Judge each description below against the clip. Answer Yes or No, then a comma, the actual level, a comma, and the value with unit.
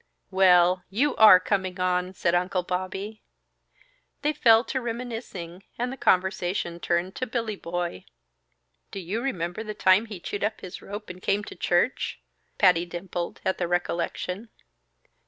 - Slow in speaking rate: No, average, 150 wpm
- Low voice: No, high, 190 Hz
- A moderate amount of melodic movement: Yes, average, 3.5 semitones